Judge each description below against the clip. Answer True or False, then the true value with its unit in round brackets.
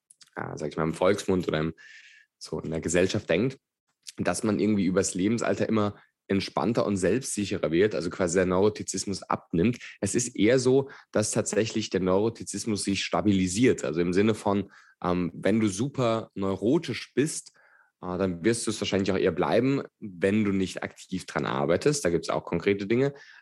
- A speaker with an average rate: True (175 wpm)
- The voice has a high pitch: False (100 Hz)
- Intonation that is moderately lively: True (3.0 semitones)